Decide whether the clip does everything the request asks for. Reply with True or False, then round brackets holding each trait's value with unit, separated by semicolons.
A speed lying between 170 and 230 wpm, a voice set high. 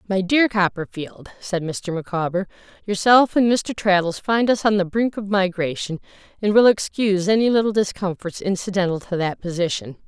False (160 wpm; 195 Hz)